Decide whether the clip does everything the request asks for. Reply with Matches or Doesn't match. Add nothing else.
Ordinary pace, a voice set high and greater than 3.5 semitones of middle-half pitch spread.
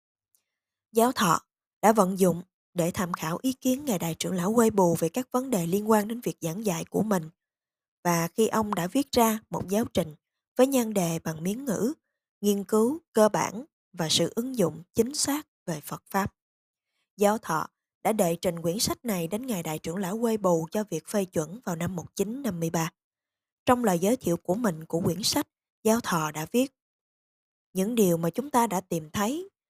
Matches